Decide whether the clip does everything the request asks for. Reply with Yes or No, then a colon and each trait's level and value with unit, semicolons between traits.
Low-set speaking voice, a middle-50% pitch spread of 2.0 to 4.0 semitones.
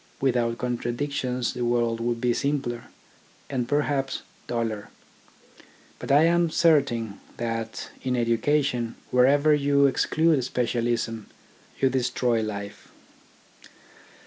Yes: low, 125 Hz; average, 3.1 semitones